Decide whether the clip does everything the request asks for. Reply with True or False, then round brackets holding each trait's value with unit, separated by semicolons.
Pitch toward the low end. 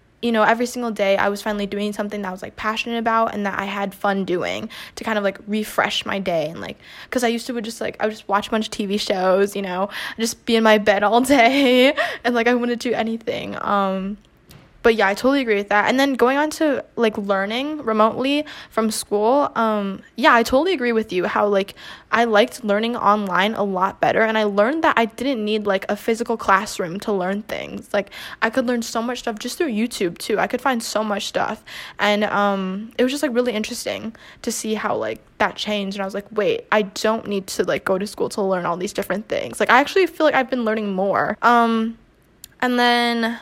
False (220 Hz)